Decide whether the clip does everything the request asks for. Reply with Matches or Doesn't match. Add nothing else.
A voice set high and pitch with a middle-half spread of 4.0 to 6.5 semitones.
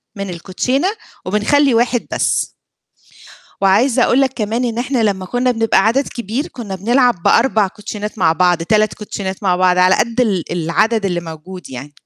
Matches